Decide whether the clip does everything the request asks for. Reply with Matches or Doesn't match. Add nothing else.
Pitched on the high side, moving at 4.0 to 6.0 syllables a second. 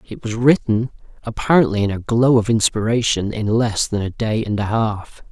Doesn't match